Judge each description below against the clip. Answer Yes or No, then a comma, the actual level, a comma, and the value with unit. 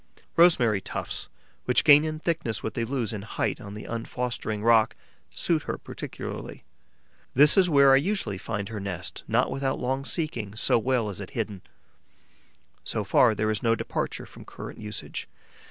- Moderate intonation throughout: Yes, average, 4.6 semitones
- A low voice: Yes, low, 115 Hz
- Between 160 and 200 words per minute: Yes, average, 170 wpm